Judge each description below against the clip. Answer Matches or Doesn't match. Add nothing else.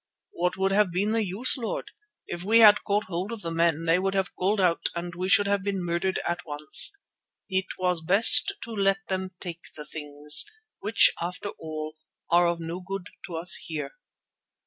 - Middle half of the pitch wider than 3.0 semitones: Doesn't match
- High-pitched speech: Doesn't match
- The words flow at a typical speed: Matches